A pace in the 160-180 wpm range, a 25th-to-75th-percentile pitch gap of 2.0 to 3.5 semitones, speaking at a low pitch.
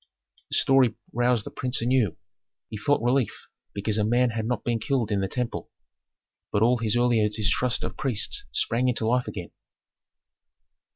Yes: average, 165 wpm; narrow, 2.6 semitones; low, 120 Hz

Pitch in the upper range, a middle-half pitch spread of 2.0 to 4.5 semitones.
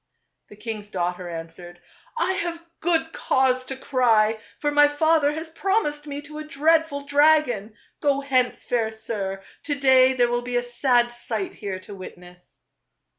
No: very high, 255 Hz; wide, 5.5 semitones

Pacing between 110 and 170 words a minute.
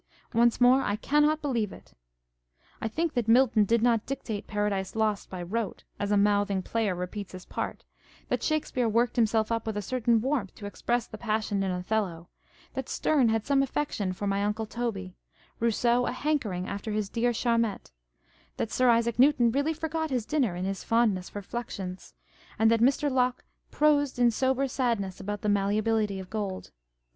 No: average, 180 wpm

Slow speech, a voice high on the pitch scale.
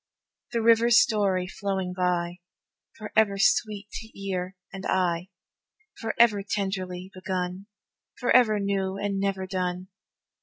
Yes: slow, 110 wpm; high, 195 Hz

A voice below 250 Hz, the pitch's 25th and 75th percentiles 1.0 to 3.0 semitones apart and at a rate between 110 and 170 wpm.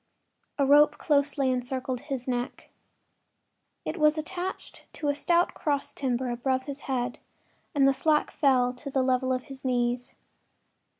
No: very high, 270 Hz; narrow, 2.6 semitones; average, 145 wpm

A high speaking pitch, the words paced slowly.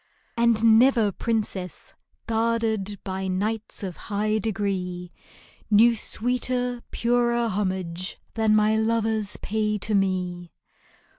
Yes: high, 215 Hz; slow, 100 wpm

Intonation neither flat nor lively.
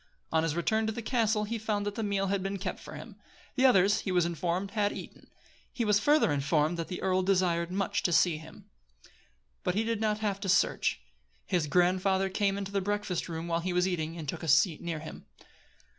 Yes: average, 3.4 semitones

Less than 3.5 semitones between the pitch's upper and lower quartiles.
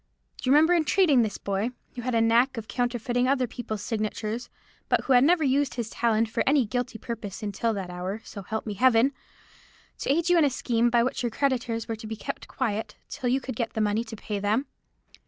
Yes: average, 3.1 semitones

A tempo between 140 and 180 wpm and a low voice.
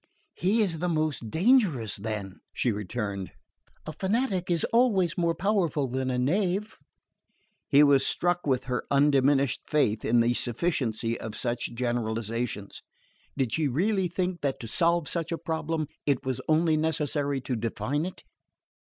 No: average, 150 wpm; medium, 145 Hz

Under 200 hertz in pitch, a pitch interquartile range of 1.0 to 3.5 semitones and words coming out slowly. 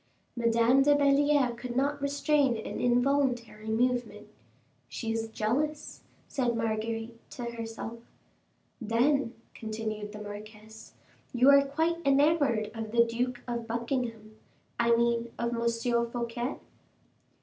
No: high, 235 Hz; average, 3.2 semitones; slow, 115 wpm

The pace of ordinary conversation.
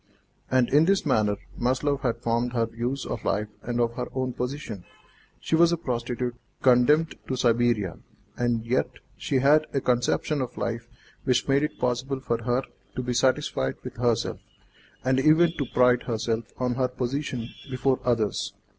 Yes: average, 165 wpm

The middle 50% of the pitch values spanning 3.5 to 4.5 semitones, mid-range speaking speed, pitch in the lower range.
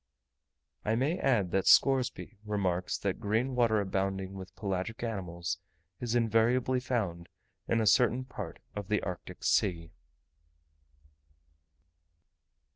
No: average, 4.1 semitones; slow, 115 wpm; low, 105 Hz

